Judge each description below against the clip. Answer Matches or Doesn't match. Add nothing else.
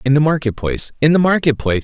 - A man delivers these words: Matches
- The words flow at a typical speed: Doesn't match